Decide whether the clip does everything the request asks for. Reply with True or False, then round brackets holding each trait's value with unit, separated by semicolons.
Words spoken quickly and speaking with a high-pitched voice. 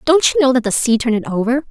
True (315 wpm; 245 Hz)